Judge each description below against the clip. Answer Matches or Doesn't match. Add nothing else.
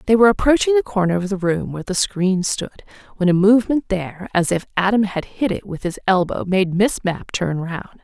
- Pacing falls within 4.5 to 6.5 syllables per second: Matches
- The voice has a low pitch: Doesn't match